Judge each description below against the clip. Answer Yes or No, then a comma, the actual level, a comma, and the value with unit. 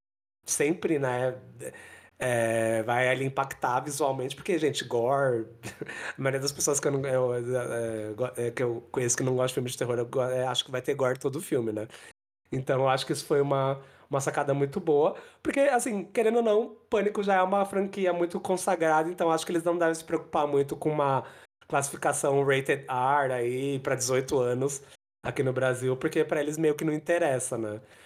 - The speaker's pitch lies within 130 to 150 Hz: Yes, medium, 140 Hz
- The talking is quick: Yes, fast, 190 wpm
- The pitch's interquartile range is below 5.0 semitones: Yes, average, 4.3 semitones